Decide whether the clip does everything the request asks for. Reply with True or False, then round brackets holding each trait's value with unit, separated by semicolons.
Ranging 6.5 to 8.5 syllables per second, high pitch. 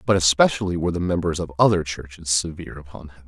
False (7.0 syllables/s; 85 Hz)